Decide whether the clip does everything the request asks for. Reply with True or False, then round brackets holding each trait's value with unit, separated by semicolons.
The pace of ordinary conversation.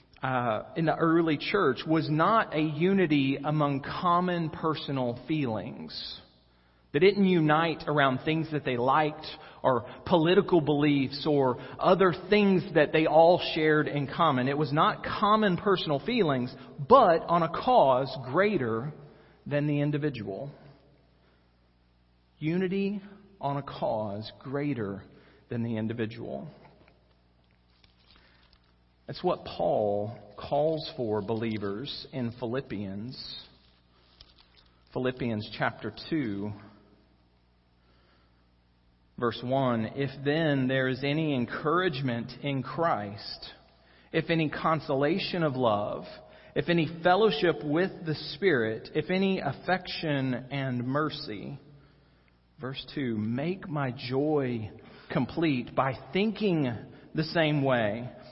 False (105 wpm)